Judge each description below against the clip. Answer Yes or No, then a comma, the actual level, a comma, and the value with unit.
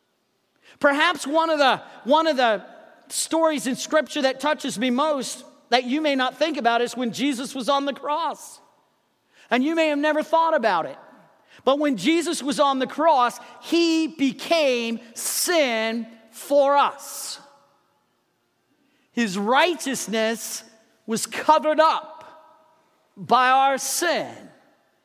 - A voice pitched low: No, very high, 280 Hz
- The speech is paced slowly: Yes, slow, 130 wpm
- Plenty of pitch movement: No, average, 4.3 semitones